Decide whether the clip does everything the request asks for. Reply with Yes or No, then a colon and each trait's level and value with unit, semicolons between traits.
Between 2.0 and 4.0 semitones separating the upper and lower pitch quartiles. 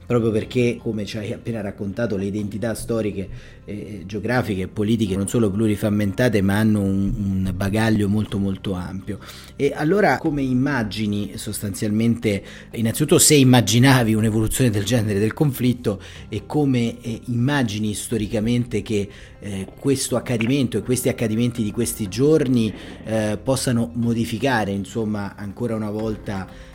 Yes: average, 2.8 semitones